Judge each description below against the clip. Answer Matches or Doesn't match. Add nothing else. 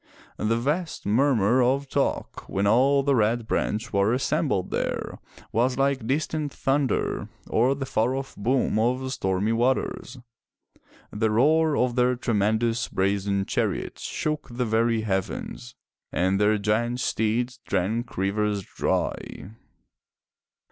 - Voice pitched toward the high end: Doesn't match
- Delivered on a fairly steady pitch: Doesn't match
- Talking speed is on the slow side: Matches